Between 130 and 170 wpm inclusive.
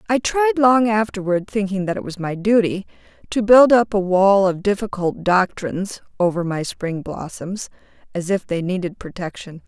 Yes: average, 165 wpm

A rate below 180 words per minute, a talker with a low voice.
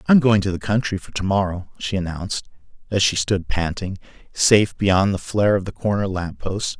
No: fast, 205 wpm; very low, 95 Hz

